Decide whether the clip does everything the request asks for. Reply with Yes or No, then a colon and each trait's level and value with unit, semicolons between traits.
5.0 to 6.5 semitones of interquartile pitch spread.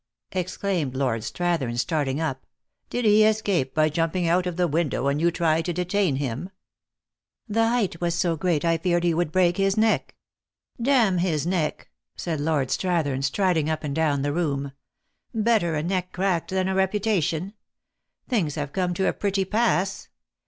No: average, 3.8 semitones